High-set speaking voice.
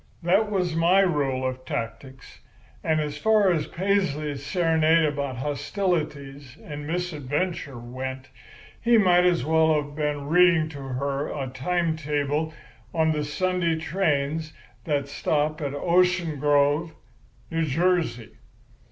No: medium, 155 Hz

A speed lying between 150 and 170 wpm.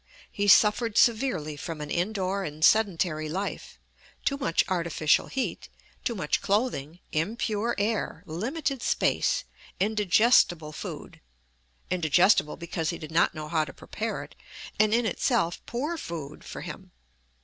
No: slow, 135 wpm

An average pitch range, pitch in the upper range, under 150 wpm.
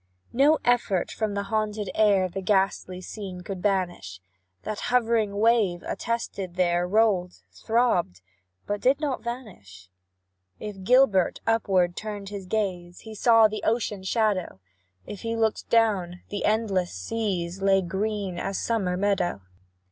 Yes: average, 3.4 semitones; high, 200 Hz; slow, 135 wpm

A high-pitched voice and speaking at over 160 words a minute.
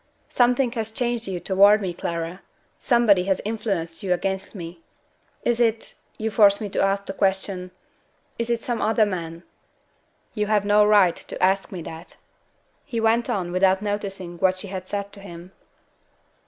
Yes: high, 200 Hz; average, 170 wpm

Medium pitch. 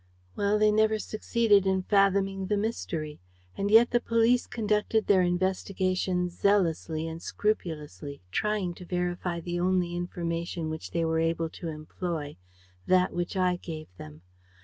Yes: medium, 180 Hz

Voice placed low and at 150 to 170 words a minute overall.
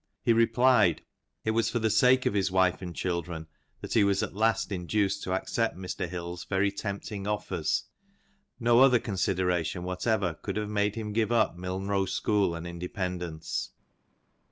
Yes: low, 100 Hz; average, 160 wpm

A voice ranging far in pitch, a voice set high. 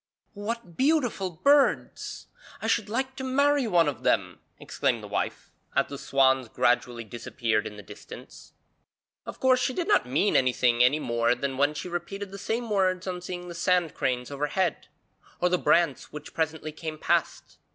No: wide, 7.7 semitones; medium, 165 Hz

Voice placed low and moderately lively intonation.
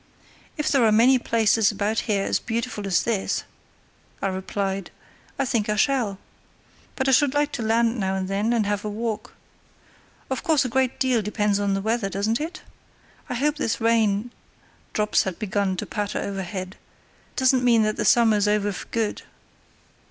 No: high, 220 Hz; average, 3.2 semitones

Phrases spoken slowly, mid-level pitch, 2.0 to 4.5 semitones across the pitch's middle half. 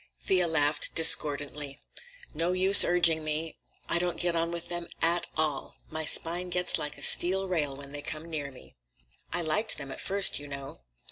No: average, 185 wpm; medium, 165 Hz; average, 3.1 semitones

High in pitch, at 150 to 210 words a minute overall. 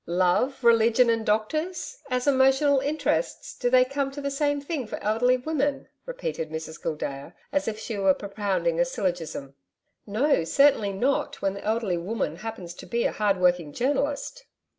Yes: high, 230 Hz; average, 165 wpm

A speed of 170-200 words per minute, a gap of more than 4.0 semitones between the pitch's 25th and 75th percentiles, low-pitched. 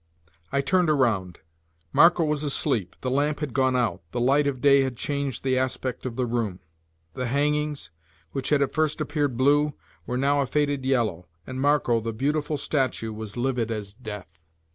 No: average, 180 wpm; average, 3.6 semitones; low, 130 Hz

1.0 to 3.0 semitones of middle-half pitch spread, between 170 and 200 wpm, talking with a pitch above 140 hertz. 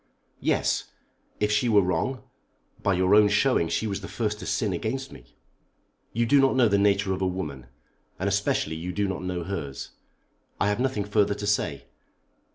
No: narrow, 2.6 semitones; average, 185 wpm; low, 100 Hz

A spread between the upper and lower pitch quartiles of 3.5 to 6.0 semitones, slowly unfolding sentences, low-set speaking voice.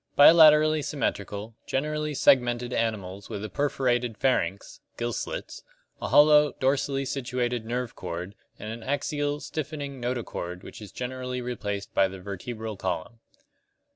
Yes: average, 5.3 semitones; slow, 130 wpm; low, 125 Hz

